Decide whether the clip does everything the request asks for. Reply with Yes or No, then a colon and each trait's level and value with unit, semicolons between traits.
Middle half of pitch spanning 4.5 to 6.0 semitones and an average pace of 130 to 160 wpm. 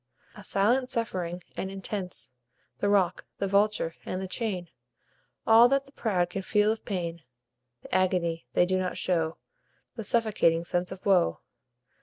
No: average, 3.1 semitones; average, 155 wpm